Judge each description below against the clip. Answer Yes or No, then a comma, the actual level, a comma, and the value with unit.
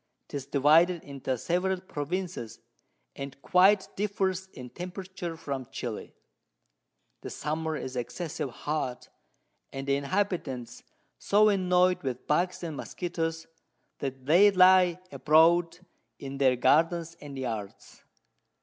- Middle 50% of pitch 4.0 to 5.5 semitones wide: Yes, average, 4.9 semitones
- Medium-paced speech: No, slow, 115 wpm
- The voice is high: No, medium, 165 Hz